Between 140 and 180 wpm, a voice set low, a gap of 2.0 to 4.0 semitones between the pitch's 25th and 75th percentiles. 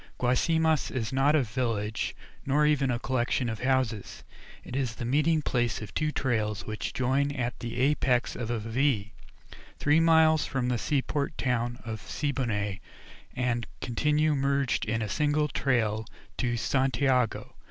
Yes: average, 150 wpm; low, 130 Hz; average, 3.5 semitones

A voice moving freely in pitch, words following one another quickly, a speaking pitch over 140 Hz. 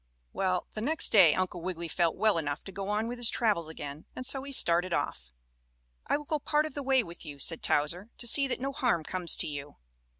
Yes: wide, 7.3 semitones; fast, 235 wpm; medium, 185 Hz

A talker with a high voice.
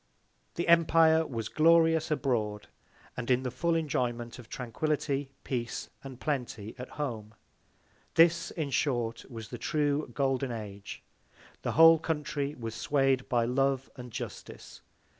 No: low, 135 Hz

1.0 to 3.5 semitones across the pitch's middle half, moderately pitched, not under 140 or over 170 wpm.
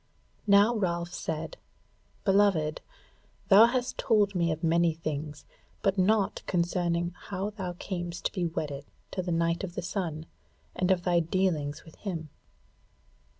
Yes: average, 2.9 semitones; medium, 175 Hz; average, 145 wpm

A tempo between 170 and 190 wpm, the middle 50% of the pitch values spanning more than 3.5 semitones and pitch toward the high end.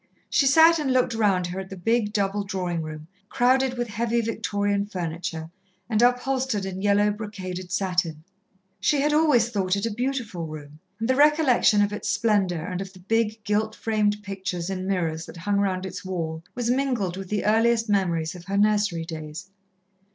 Yes: average, 180 wpm; average, 4.0 semitones; high, 205 Hz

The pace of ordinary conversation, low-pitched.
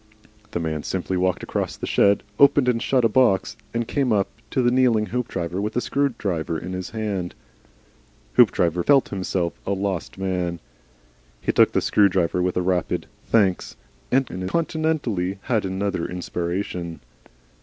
Yes: average, 150 wpm; very low, 95 Hz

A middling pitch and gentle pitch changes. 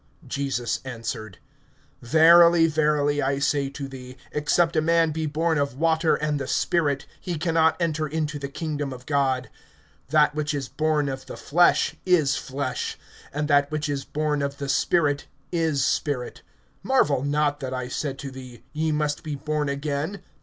Yes: medium, 145 Hz; narrow, 2.3 semitones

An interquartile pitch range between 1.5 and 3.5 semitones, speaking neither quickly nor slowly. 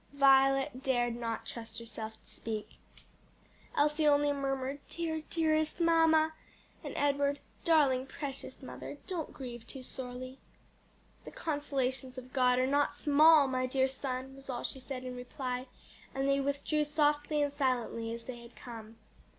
Yes: narrow, 2.5 semitones; average, 150 wpm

